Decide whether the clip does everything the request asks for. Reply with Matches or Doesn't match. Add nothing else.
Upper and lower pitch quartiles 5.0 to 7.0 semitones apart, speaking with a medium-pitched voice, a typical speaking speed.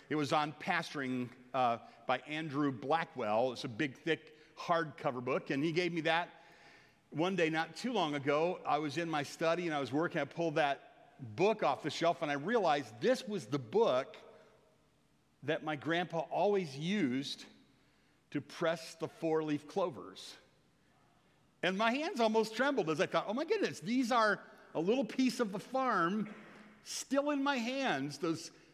Matches